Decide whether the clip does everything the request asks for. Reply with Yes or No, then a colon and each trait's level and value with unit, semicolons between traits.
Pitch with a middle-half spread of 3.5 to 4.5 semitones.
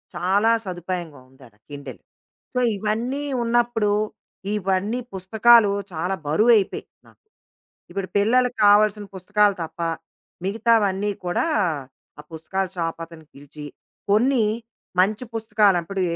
Yes: average, 4.0 semitones